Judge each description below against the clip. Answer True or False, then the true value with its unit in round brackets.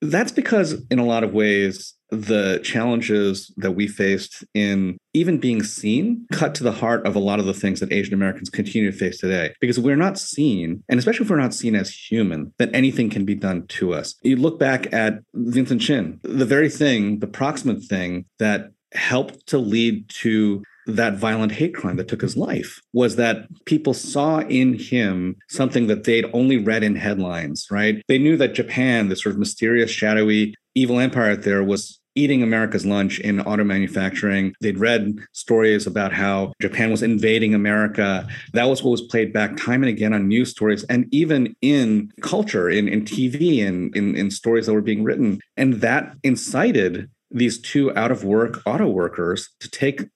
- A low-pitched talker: True (110 Hz)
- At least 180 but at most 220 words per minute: True (190 wpm)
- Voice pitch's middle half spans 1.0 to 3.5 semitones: False (4.1 semitones)